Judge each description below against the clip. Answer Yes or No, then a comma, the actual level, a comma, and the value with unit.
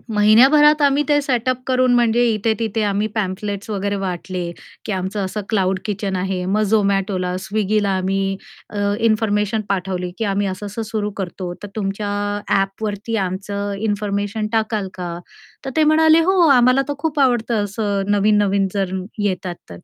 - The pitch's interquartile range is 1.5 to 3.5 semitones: Yes, narrow, 2.6 semitones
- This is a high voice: Yes, high, 205 Hz